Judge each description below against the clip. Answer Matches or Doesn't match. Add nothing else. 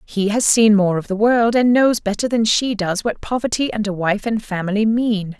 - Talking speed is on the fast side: Matches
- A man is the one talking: Doesn't match